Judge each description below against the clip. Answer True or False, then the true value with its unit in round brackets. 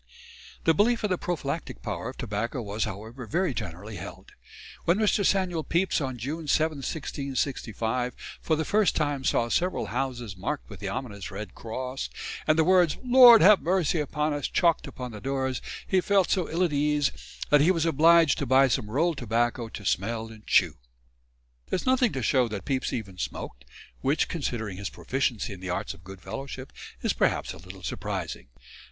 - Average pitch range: False (6.7 semitones)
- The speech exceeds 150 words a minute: True (185 wpm)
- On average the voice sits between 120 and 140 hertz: True (135 Hz)